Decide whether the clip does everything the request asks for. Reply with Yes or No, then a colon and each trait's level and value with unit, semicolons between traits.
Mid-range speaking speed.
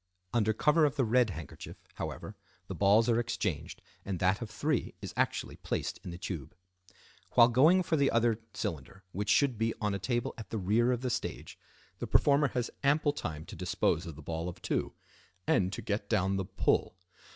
Yes: average, 195 wpm